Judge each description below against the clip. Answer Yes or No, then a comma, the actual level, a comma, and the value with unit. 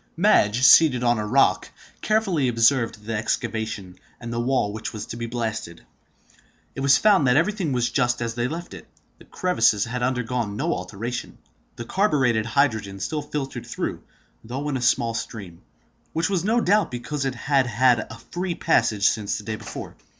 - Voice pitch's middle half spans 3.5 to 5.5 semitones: Yes, average, 4.7 semitones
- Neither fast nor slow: Yes, average, 180 wpm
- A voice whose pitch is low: Yes, low, 120 Hz